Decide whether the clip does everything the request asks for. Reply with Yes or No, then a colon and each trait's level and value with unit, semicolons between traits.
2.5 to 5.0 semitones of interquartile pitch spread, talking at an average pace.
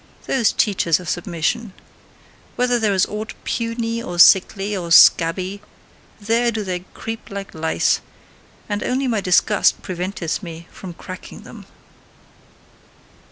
No: average, 4.2 semitones; slow, 125 wpm